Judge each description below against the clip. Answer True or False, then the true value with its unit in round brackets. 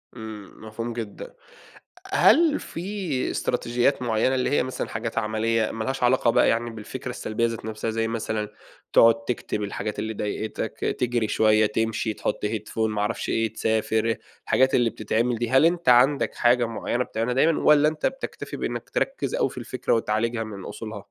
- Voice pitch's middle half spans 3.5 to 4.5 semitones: False (2.5 semitones)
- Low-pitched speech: True (115 Hz)